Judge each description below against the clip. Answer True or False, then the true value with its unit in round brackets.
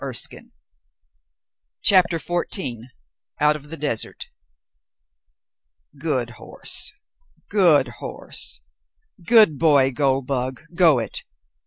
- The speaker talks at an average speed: False (85 wpm)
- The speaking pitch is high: False (150 Hz)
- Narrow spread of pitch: False (4.3 semitones)